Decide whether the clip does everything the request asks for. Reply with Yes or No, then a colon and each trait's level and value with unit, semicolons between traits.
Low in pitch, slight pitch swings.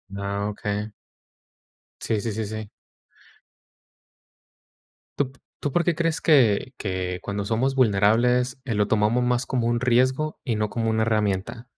No: low, 115 Hz; average, 3.6 semitones